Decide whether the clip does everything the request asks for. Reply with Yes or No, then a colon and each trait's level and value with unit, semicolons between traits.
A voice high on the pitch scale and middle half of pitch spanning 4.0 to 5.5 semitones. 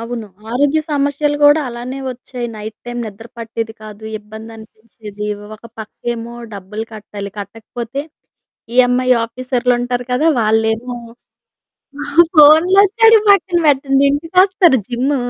Yes: high, 245 Hz; average, 4.4 semitones